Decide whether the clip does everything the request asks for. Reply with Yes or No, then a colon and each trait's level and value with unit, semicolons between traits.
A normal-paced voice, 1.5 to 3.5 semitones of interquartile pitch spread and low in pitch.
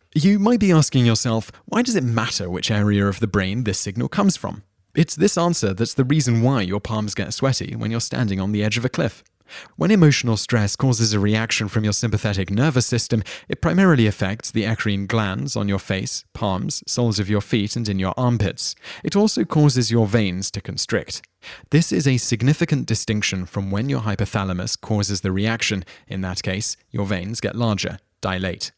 No: average, 195 wpm; average, 4.1 semitones; low, 110 Hz